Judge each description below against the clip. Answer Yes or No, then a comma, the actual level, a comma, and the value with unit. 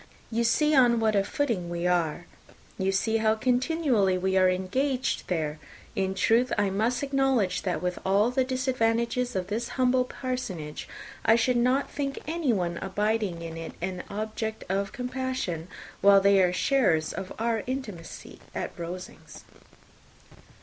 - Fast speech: No, average, 150 wpm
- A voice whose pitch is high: Yes, high, 220 Hz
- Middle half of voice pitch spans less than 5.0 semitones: No, average, 5.3 semitones